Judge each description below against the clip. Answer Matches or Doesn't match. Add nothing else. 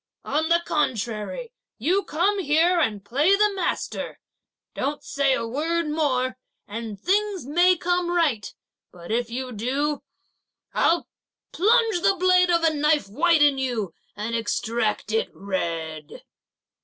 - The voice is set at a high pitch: Matches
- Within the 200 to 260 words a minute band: Doesn't match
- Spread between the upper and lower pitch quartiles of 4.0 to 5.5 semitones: Doesn't match